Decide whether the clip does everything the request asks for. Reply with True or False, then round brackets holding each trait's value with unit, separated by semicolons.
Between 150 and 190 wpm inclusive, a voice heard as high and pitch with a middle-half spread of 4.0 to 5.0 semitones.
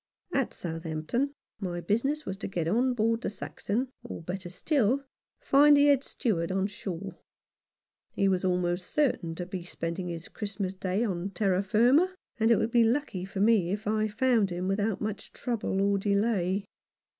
True (175 wpm; 200 Hz; 4.3 semitones)